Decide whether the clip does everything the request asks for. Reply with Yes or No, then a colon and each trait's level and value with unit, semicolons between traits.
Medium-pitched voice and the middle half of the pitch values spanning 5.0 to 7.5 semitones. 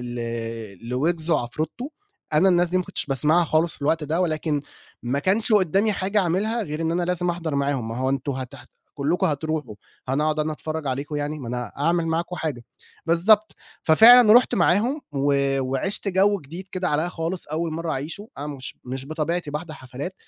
No: medium, 155 Hz; average, 4.2 semitones